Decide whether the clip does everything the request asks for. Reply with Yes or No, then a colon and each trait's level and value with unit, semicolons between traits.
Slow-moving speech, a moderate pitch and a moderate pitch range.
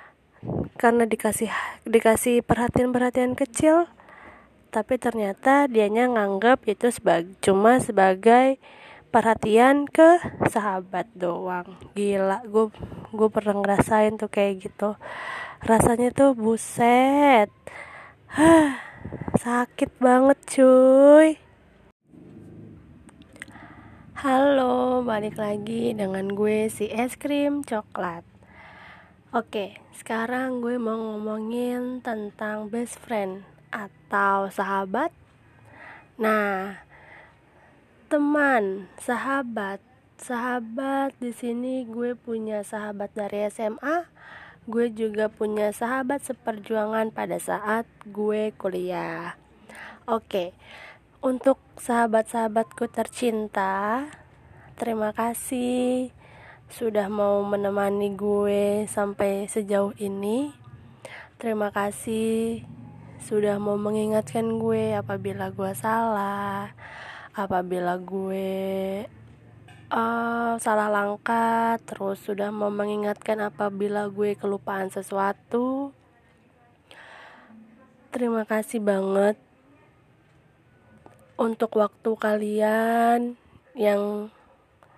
No: slow, 80 wpm; high, 220 Hz; average, 3.1 semitones